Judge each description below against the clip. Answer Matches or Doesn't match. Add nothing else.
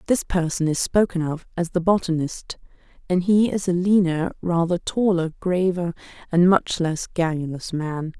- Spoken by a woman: Matches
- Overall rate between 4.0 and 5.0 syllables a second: Matches